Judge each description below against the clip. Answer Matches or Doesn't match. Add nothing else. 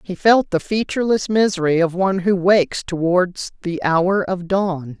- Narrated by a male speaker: Doesn't match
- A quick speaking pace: Doesn't match